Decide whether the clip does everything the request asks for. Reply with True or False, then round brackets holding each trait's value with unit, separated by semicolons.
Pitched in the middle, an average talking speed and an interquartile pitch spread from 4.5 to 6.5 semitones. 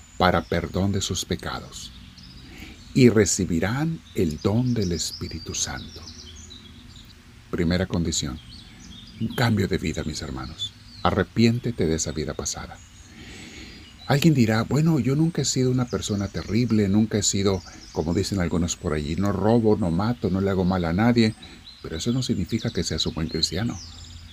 False (95 Hz; 155 wpm; 5.5 semitones)